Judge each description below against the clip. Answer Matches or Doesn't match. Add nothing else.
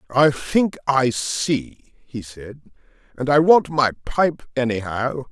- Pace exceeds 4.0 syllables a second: Doesn't match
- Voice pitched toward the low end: Matches